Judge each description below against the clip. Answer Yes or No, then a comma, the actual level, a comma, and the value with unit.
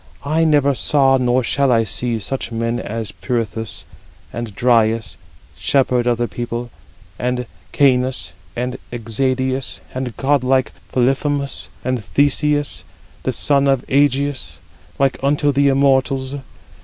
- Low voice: Yes, low, 130 Hz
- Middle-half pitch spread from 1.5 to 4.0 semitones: Yes, narrow, 2.5 semitones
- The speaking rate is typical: No, slow, 130 wpm